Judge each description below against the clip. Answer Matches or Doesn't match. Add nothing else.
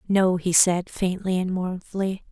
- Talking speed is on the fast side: Doesn't match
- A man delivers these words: Doesn't match